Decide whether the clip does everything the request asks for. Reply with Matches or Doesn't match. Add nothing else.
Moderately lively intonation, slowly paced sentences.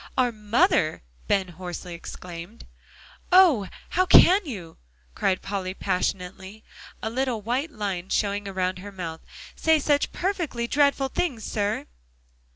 Doesn't match